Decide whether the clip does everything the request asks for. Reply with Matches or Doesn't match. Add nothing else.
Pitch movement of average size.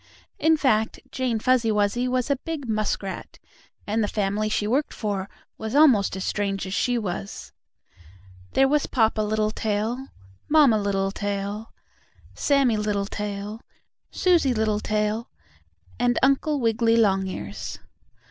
Matches